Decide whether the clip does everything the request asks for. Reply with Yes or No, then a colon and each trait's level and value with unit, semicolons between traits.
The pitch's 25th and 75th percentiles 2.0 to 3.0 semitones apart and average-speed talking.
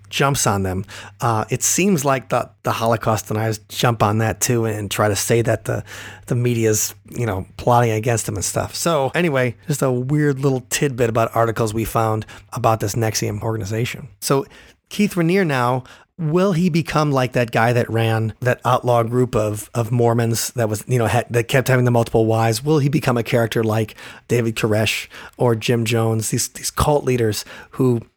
Yes: average, 2.7 semitones; average, 190 wpm